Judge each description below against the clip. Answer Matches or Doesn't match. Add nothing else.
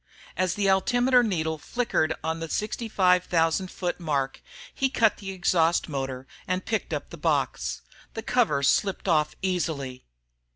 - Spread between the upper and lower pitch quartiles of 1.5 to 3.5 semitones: Doesn't match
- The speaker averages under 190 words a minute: Matches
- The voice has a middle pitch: Matches